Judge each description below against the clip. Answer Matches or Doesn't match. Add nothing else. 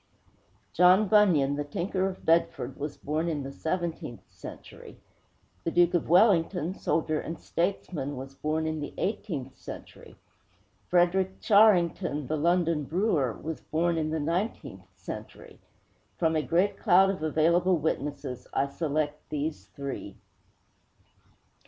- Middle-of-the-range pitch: Matches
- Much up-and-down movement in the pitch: Doesn't match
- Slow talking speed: Matches